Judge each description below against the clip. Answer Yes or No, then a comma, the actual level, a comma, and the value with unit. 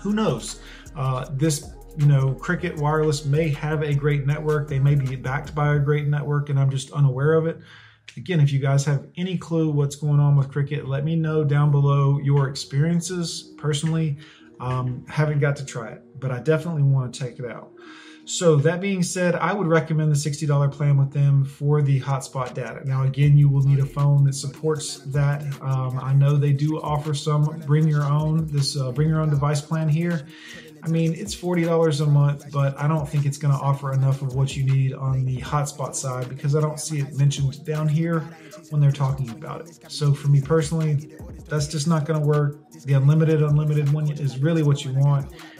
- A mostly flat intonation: Yes, narrow, 2.1 semitones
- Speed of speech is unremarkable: No, fast, 210 wpm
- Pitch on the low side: No, medium, 145 Hz